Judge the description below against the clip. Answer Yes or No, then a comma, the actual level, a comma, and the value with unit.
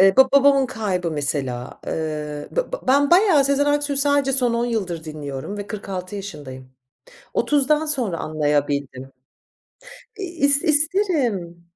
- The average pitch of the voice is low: No, high, 215 Hz